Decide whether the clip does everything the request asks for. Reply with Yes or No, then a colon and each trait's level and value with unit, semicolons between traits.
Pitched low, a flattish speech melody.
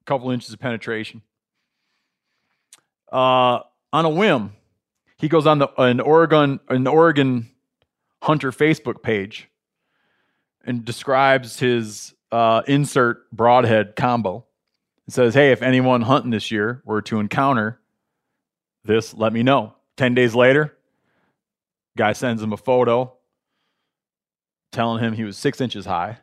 No: low, 125 Hz; average, 3.4 semitones